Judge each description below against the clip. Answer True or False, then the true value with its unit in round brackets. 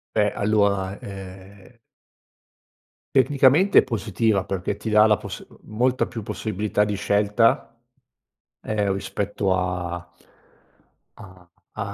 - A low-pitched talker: True (100 Hz)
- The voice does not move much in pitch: True (2.2 semitones)